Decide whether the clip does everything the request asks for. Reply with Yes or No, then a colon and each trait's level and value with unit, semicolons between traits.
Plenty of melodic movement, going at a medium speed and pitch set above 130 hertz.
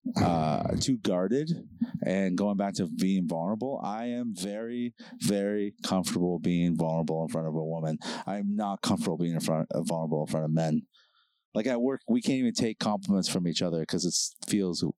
No: wide, 6.7 semitones; average, 195 wpm; very low, 95 Hz